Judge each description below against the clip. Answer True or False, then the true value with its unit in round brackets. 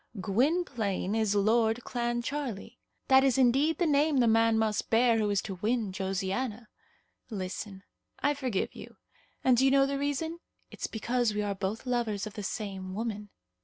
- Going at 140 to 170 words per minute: True (165 wpm)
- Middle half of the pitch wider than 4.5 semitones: False (4.2 semitones)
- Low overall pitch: False (225 Hz)